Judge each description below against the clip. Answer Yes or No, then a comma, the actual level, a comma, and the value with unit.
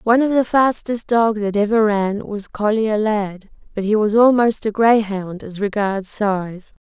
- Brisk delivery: No, average, 175 wpm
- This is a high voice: Yes, high, 215 Hz